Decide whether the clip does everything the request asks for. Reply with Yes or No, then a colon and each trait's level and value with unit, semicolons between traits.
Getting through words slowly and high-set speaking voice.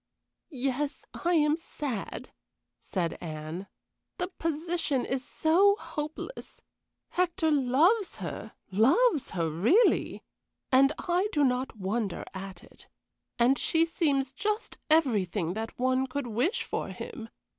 Yes: slow, 120 wpm; very high, 275 Hz